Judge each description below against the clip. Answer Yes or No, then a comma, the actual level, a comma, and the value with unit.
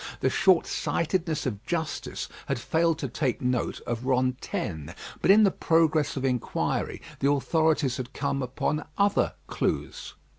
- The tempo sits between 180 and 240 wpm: No, average, 140 wpm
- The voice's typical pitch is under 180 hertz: Yes, medium, 140 Hz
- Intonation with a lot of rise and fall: No, average, 4.3 semitones